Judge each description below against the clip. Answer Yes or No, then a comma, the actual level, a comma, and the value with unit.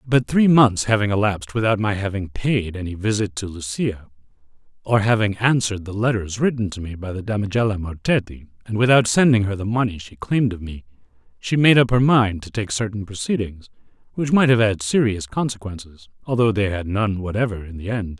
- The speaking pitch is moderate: No, low, 105 Hz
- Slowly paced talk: No, average, 190 wpm